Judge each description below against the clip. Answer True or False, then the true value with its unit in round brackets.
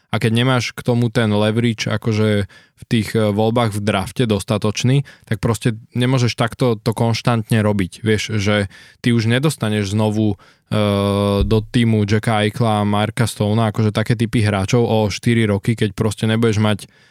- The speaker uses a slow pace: False (160 wpm)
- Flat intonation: True (2.1 semitones)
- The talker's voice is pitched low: True (110 Hz)